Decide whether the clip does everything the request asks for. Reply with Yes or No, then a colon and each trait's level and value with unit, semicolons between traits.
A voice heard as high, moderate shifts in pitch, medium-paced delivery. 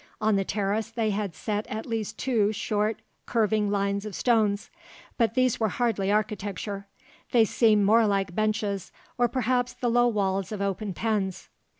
No: high, 215 Hz; narrow, 2.2 semitones; average, 165 wpm